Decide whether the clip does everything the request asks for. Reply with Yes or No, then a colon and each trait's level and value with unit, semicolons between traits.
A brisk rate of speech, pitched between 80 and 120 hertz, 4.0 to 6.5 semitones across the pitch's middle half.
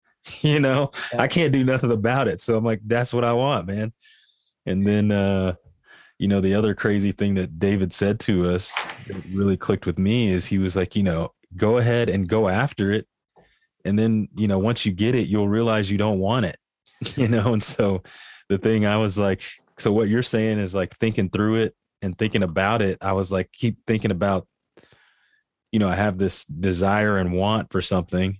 No: fast, 210 wpm; low, 105 Hz; average, 2.8 semitones